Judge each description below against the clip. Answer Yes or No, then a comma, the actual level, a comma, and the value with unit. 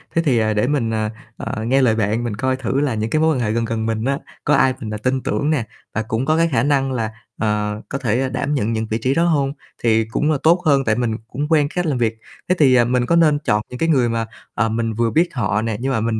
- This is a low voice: Yes, low, 120 Hz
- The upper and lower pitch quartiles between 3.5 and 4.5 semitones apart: Yes, average, 4.1 semitones